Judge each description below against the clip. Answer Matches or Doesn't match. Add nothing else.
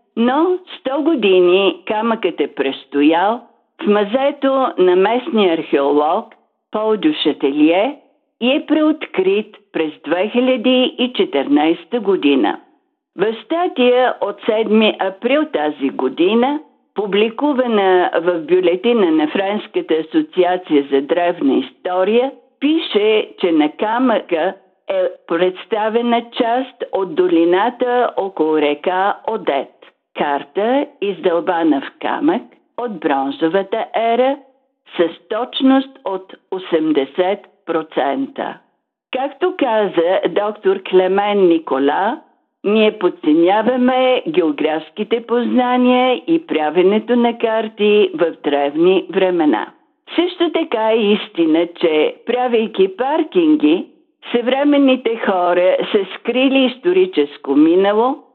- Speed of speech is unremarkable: Doesn't match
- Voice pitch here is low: Doesn't match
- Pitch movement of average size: Doesn't match